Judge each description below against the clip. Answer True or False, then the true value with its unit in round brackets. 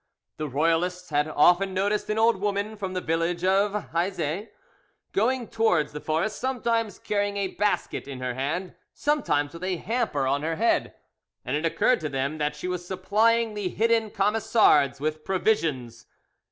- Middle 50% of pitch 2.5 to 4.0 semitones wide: False (5.6 semitones)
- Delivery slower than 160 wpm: False (165 wpm)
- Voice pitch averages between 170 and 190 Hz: True (185 Hz)